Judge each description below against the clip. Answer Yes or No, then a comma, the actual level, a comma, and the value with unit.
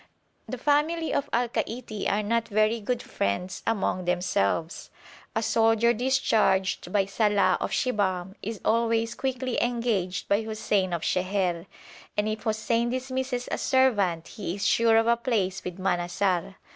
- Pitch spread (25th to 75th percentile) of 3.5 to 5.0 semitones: Yes, average, 4.0 semitones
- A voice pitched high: Yes, high, 215 Hz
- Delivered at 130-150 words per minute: Yes, average, 145 wpm